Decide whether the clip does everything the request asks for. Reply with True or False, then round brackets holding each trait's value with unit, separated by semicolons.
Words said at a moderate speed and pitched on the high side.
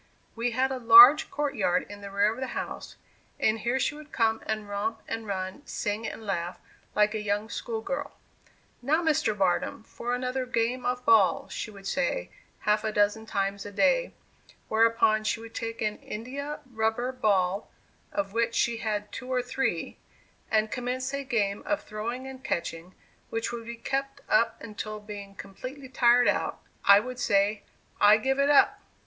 True (180 wpm; 225 Hz)